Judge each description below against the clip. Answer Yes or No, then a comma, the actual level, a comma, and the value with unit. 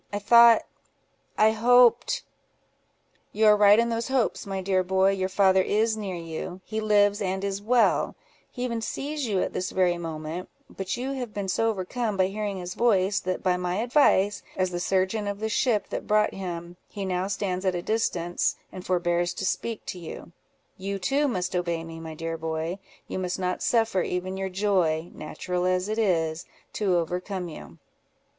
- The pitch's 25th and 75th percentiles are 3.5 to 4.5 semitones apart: No, average, 3.1 semitones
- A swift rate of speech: No, average, 185 wpm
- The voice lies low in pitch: No, high, 190 Hz